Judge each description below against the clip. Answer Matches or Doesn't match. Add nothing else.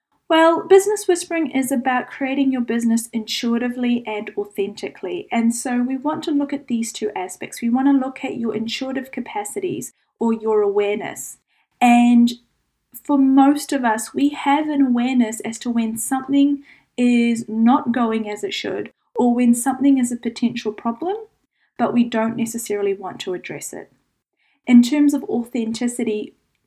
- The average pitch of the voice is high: Matches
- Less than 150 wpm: Doesn't match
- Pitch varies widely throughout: Doesn't match